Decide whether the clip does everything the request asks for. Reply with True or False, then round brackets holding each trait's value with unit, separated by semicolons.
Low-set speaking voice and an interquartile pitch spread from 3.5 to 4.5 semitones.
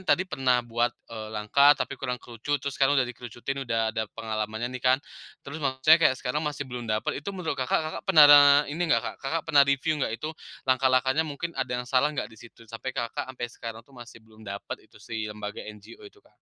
True (130 Hz; 4.0 semitones)